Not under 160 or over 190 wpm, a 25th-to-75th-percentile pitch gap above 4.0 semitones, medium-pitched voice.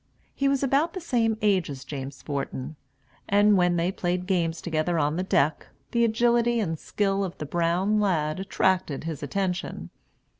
Yes: average, 165 wpm; average, 4.9 semitones; medium, 180 Hz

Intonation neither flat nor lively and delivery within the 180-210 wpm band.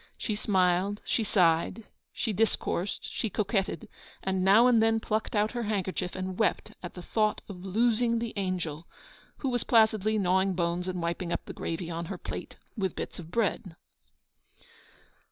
No: average, 3.5 semitones; average, 165 wpm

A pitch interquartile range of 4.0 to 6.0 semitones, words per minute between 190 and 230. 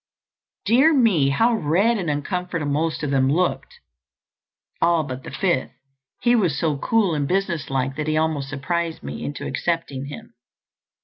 No: average, 4.8 semitones; average, 150 wpm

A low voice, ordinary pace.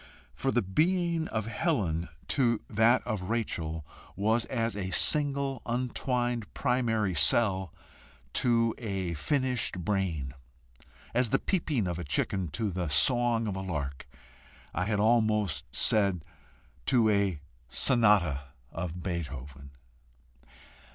No: low, 105 Hz; slow, 115 wpm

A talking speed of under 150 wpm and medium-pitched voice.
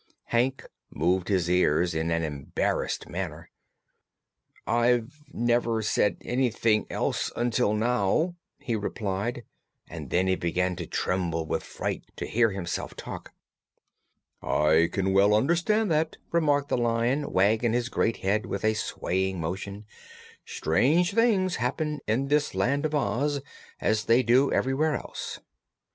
No: slow, 135 wpm; low, 115 Hz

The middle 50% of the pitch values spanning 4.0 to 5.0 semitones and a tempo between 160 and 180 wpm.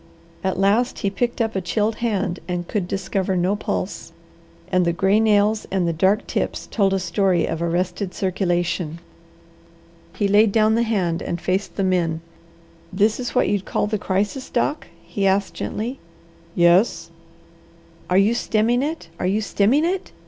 No: average, 3.2 semitones; average, 165 wpm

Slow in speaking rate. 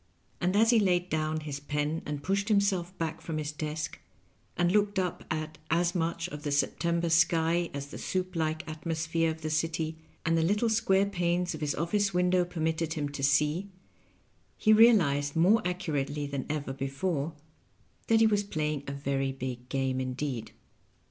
No: average, 175 wpm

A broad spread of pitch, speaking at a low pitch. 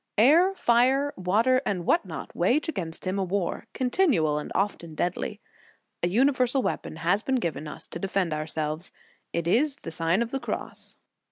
No: wide, 7.4 semitones; high, 195 Hz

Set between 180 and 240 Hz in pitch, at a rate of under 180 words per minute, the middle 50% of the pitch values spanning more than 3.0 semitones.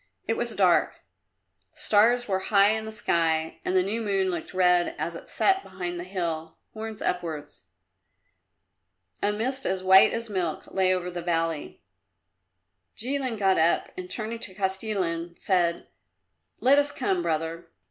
Yes: high, 190 Hz; average, 155 wpm; average, 4.1 semitones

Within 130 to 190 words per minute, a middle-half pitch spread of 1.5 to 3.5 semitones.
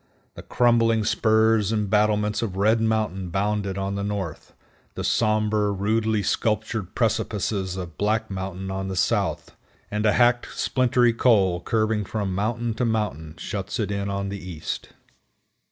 Yes: average, 155 wpm; narrow, 2.4 semitones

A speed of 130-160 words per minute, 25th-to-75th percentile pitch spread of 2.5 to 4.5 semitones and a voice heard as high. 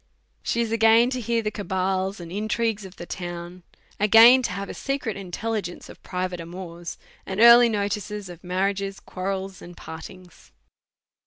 Yes: average, 150 wpm; average, 3.5 semitones; high, 195 Hz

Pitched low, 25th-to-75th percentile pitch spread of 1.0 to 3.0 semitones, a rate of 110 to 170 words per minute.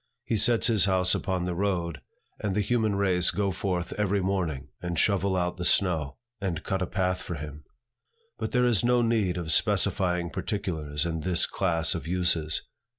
No: very low, 90 Hz; average, 2.7 semitones; average, 180 wpm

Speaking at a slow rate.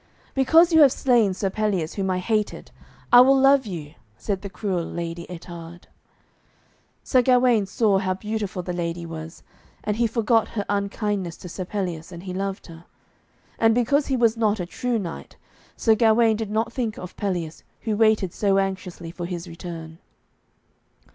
No: average, 170 wpm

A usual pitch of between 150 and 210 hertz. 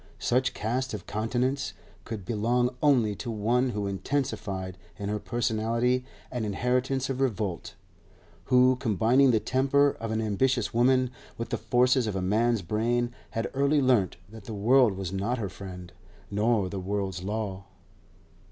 No: low, 115 Hz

